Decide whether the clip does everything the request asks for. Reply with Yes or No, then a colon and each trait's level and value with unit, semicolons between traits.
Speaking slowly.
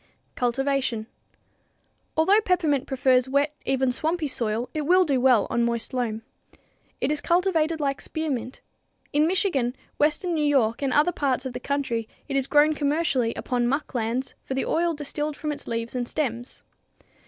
No: average, 165 wpm